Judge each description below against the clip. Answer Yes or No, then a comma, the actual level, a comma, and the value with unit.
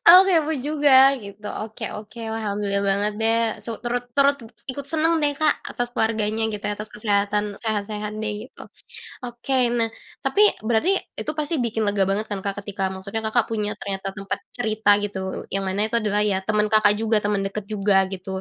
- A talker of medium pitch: No, high, 215 Hz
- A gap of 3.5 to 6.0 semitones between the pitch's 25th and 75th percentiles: No, narrow, 2.4 semitones